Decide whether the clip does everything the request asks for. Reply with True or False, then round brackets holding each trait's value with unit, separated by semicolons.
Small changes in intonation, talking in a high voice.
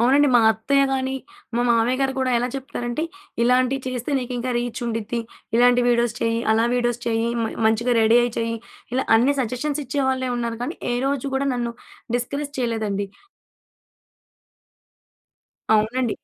True (2.2 semitones; 245 Hz)